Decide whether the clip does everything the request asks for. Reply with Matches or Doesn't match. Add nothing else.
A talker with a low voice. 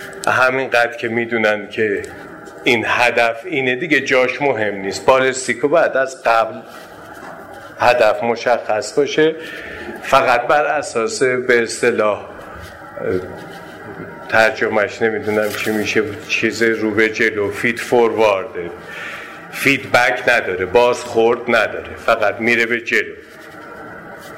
Matches